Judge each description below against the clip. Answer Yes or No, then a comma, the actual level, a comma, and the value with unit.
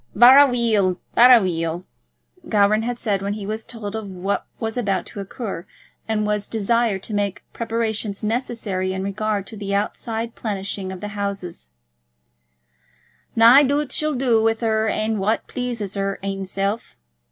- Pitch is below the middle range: No, high, 215 Hz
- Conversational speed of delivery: Yes, average, 150 wpm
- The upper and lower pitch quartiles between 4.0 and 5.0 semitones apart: No, average, 2.7 semitones